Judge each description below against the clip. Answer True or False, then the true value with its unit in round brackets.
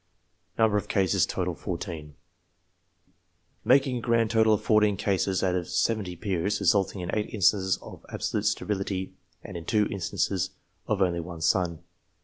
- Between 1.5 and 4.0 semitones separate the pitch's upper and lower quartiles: True (3.1 semitones)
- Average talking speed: False (130 wpm)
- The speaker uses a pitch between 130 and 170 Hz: False (95 Hz)